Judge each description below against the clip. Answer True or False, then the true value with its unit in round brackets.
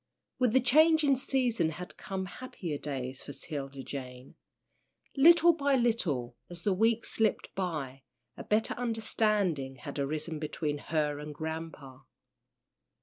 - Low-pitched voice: False (165 Hz)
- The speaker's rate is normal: False (130 wpm)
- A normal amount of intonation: False (8.4 semitones)